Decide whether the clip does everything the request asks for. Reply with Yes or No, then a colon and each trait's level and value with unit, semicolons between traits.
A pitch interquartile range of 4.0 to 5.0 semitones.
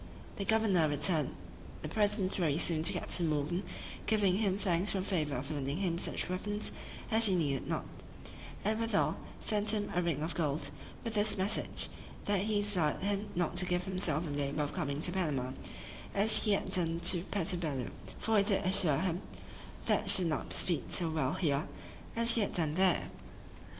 Yes: average, 4.6 semitones